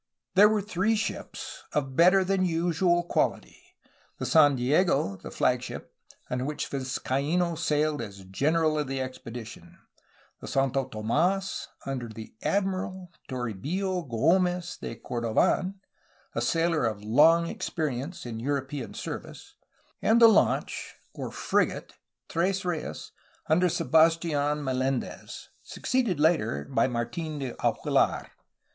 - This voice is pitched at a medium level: Yes, medium, 155 Hz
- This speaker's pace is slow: Yes, slow, 125 wpm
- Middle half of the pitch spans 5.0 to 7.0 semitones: Yes, wide, 5.5 semitones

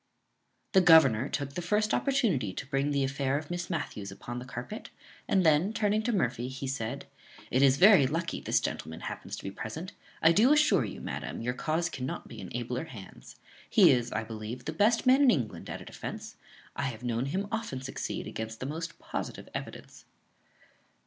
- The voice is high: No, medium, 140 Hz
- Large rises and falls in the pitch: Yes, wide, 6.6 semitones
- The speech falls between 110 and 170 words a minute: No, average, 195 wpm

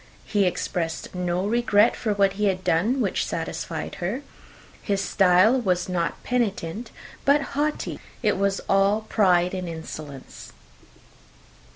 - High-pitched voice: Yes, high, 195 Hz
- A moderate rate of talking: No, slow, 130 wpm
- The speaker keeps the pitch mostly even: No, average, 3.5 semitones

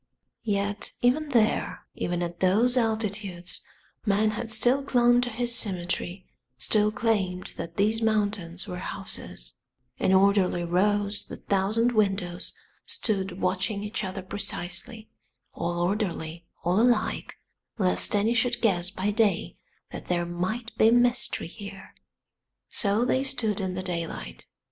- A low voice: No, high, 205 Hz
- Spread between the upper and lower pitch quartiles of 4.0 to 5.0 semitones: No, average, 3.6 semitones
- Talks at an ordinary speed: No, slow, 130 wpm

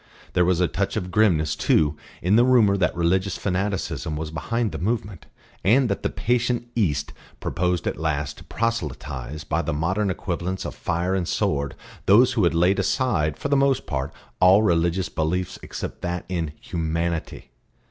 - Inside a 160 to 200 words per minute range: Yes, average, 170 wpm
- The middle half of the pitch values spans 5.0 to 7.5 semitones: No, average, 4.5 semitones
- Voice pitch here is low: Yes, very low, 90 Hz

